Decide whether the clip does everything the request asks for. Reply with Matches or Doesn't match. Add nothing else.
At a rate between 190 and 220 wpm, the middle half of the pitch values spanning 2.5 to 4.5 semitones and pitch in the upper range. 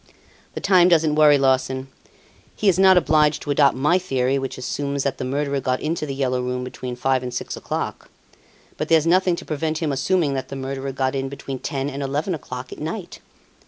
Doesn't match